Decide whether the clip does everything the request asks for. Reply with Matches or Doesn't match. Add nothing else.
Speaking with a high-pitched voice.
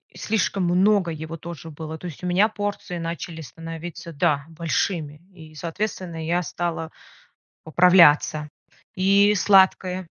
Doesn't match